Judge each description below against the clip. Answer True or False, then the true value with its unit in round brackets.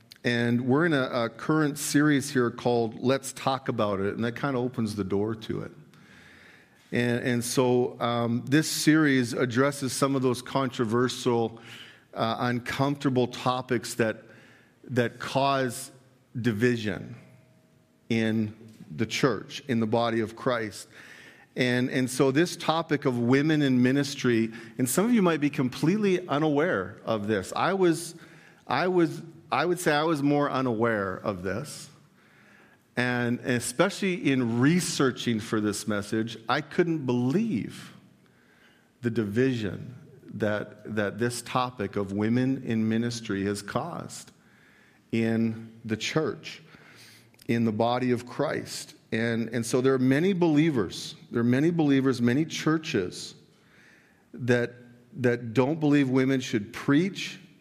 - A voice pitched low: True (125 Hz)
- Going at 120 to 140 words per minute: True (135 wpm)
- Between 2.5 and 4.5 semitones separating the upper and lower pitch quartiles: True (3.6 semitones)